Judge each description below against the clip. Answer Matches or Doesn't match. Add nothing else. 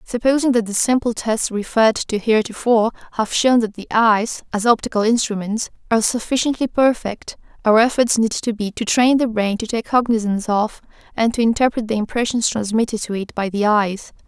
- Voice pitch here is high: Matches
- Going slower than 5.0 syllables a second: Doesn't match